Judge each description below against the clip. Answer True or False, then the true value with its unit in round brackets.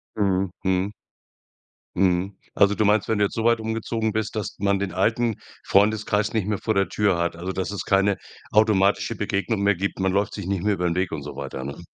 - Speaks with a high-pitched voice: False (100 Hz)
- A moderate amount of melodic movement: False (2.2 semitones)